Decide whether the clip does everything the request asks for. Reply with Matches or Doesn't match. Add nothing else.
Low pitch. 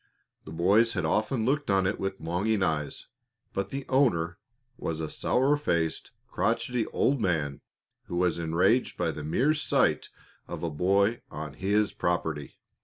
Matches